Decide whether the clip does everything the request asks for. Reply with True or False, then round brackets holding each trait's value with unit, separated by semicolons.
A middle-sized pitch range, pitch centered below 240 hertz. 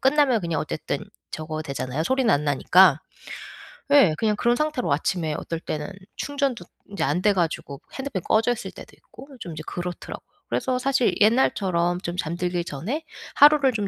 False (7.7 semitones; 190 Hz)